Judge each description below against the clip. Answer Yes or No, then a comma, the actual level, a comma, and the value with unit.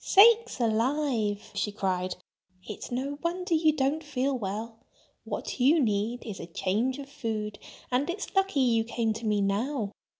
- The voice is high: Yes, high, 245 Hz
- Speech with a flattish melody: No, average, 5.3 semitones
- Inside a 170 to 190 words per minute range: No, average, 160 wpm